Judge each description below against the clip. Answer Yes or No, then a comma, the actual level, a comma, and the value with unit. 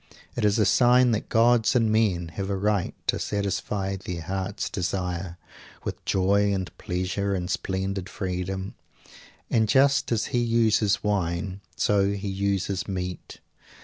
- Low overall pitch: Yes, low, 100 Hz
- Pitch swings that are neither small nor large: No, narrow, 2.3 semitones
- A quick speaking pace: No, average, 145 wpm